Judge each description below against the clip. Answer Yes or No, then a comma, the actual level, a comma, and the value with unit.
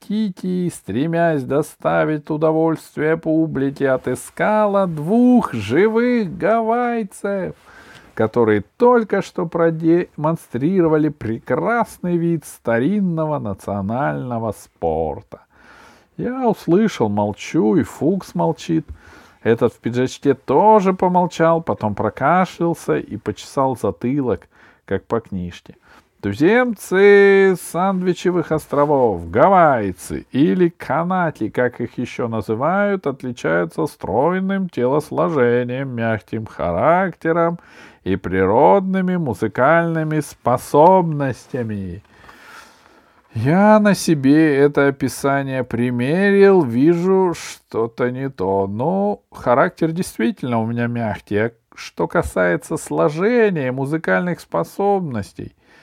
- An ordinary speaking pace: No, slow, 85 wpm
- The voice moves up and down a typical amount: No, wide, 7.5 semitones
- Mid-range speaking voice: Yes, medium, 155 Hz